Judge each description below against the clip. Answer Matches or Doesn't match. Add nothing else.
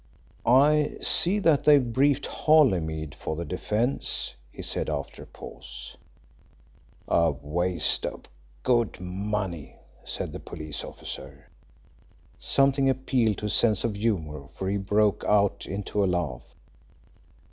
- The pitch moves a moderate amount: Doesn't match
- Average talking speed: Doesn't match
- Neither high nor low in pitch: Doesn't match